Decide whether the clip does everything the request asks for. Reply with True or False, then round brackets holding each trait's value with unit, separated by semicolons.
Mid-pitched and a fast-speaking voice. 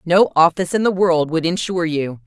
True (170 Hz; 210 wpm)